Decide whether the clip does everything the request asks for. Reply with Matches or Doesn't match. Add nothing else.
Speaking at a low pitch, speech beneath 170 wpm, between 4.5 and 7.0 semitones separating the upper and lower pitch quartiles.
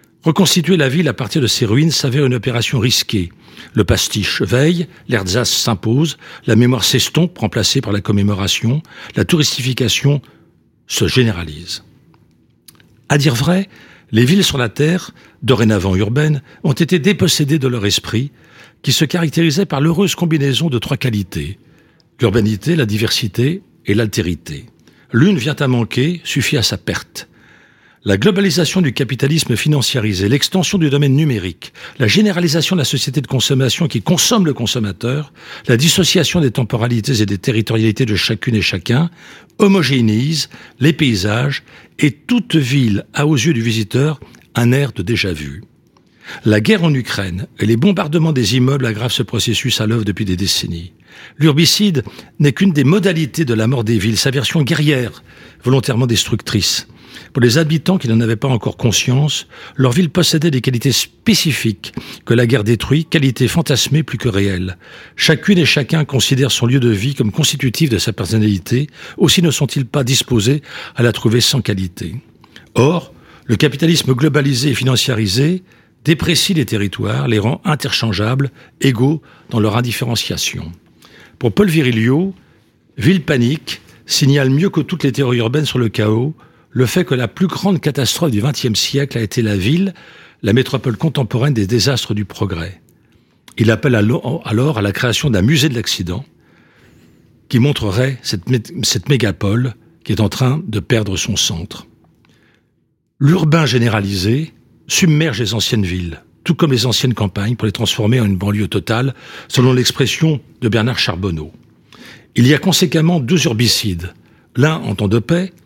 Matches